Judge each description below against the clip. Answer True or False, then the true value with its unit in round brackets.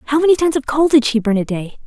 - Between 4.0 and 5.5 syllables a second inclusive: False (6.3 syllables/s)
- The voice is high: True (270 Hz)